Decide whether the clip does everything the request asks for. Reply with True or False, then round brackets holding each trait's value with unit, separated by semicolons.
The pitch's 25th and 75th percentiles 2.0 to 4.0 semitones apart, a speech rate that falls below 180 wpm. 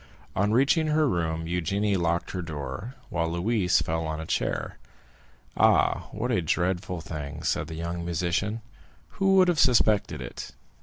False (5.0 semitones; 155 wpm)